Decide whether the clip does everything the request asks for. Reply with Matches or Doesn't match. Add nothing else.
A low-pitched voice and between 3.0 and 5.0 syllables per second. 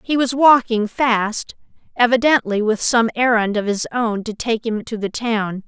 Doesn't match